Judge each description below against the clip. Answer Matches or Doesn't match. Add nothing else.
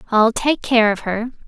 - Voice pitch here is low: Doesn't match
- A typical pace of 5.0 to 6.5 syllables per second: Doesn't match